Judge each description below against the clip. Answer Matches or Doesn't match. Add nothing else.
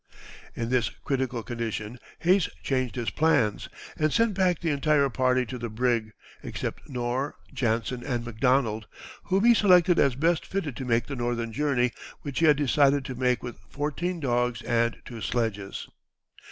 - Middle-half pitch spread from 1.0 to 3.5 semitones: Doesn't match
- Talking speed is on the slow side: Doesn't match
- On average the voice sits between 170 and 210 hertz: Doesn't match